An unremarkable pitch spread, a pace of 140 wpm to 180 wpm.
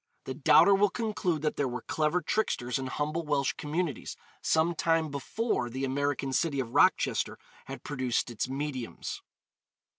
Yes: average, 3.9 semitones; average, 150 wpm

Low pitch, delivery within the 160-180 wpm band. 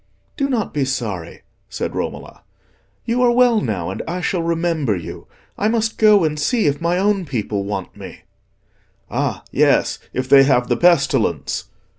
No: medium, 165 Hz; average, 165 wpm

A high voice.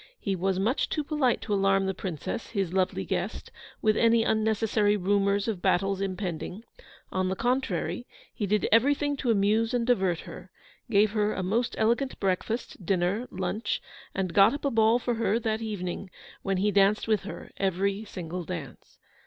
Yes: high, 205 Hz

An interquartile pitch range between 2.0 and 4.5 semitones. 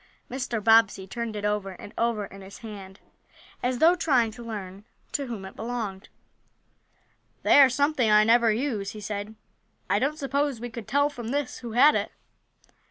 Yes: average, 3.8 semitones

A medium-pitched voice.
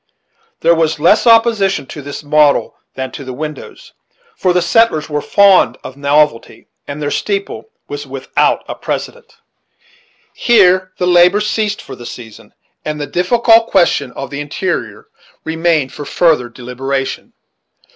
Yes: medium, 155 Hz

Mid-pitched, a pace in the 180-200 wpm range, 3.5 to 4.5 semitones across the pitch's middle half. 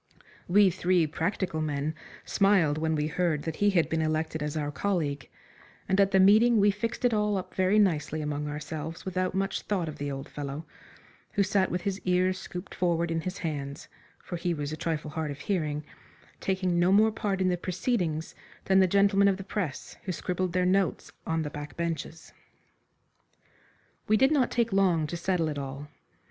Yes: medium, 175 Hz; average, 190 wpm; average, 3.8 semitones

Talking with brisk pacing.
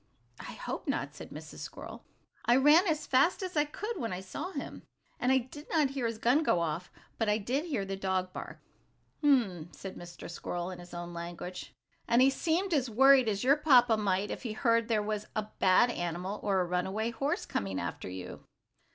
Yes: fast, 210 wpm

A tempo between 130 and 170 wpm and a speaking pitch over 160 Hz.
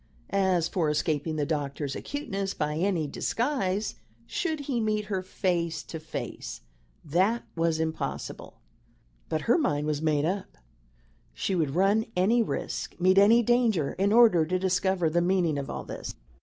Yes: average, 155 wpm; medium, 185 Hz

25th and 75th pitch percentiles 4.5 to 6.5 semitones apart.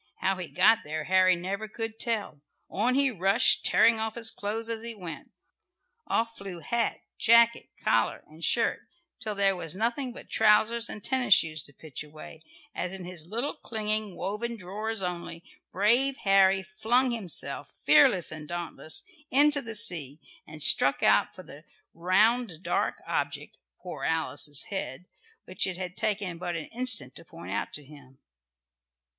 Yes: average, 5.1 semitones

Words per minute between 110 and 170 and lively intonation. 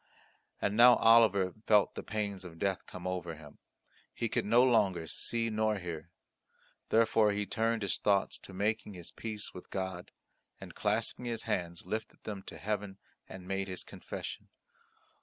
No: average, 160 wpm; average, 3.1 semitones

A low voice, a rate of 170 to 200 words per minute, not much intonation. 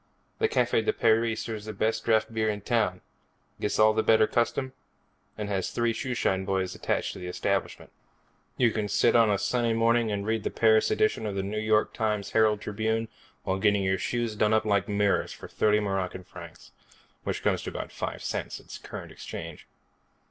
Yes: low, 110 Hz; average, 190 wpm; narrow, 2.0 semitones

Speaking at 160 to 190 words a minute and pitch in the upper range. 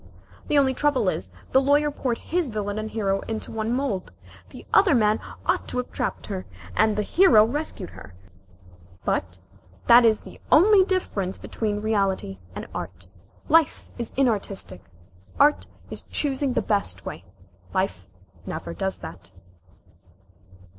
No: average, 145 wpm; high, 220 Hz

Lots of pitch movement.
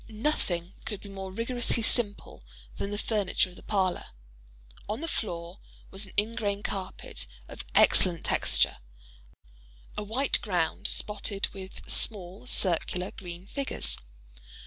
No: average, 3.5 semitones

